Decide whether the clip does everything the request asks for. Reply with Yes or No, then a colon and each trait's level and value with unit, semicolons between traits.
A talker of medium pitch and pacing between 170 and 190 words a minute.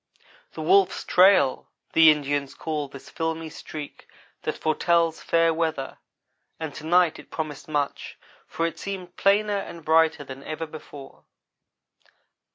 No: medium, 160 Hz; slow, 135 wpm